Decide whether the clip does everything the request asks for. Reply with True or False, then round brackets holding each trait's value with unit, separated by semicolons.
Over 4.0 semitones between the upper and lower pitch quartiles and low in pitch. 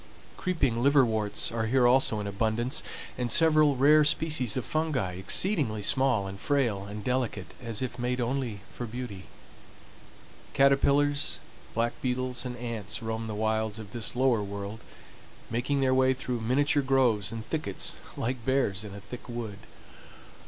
False (3.6 semitones; 120 Hz)